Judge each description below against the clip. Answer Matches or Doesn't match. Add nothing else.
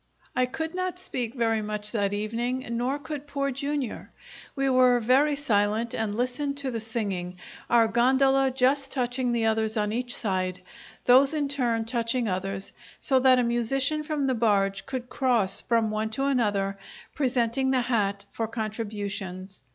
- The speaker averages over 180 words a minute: Doesn't match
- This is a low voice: Doesn't match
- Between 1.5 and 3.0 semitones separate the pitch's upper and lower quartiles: Doesn't match